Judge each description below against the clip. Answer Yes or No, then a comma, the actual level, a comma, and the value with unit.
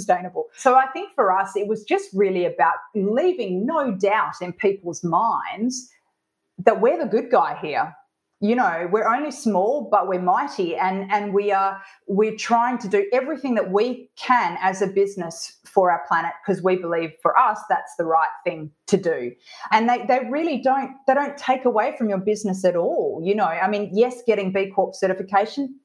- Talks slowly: No, average, 190 wpm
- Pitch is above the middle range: Yes, high, 205 Hz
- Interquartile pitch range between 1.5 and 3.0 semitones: No, average, 4.6 semitones